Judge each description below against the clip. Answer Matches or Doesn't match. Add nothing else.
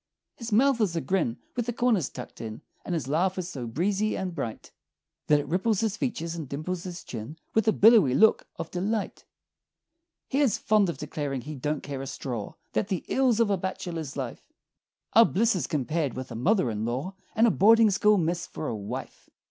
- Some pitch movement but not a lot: Doesn't match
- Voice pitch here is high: Doesn't match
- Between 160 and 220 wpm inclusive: Matches